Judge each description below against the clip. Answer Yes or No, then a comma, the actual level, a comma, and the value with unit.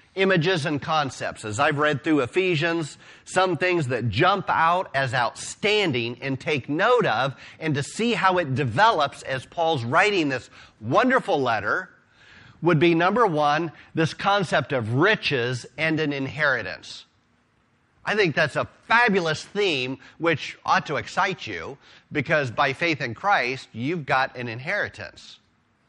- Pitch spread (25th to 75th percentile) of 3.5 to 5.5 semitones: Yes, average, 4.9 semitones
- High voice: No, medium, 155 Hz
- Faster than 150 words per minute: No, average, 145 wpm